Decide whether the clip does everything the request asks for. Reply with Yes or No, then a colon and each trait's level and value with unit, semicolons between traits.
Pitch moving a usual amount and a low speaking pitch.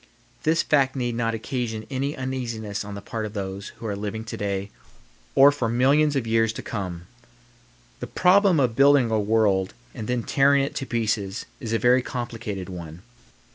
Yes: average, 4.2 semitones; low, 115 Hz